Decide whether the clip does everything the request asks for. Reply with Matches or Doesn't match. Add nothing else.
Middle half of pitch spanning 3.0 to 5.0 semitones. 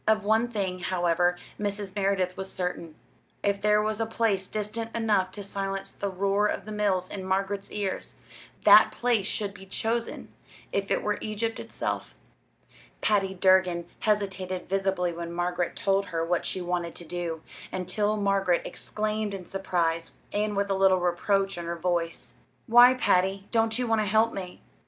Doesn't match